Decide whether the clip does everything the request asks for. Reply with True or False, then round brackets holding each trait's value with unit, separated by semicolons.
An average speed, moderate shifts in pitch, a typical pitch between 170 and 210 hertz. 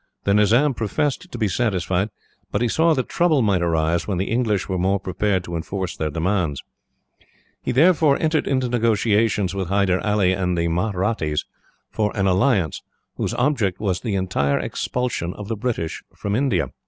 False (170 wpm; 4.9 semitones; 100 Hz)